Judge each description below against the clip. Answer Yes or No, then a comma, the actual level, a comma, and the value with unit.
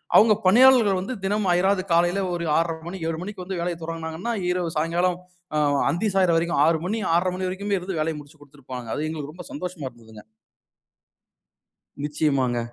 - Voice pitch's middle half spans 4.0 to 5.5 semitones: No, average, 3.3 semitones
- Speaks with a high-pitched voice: No, medium, 175 Hz